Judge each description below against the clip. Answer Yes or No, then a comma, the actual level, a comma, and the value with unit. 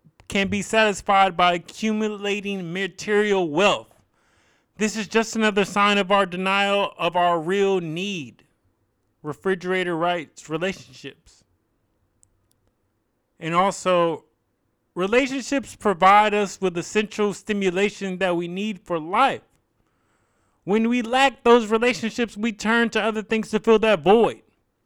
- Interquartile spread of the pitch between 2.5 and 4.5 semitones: No, average, 4.9 semitones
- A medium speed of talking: No, slow, 120 wpm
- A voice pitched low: No, high, 195 Hz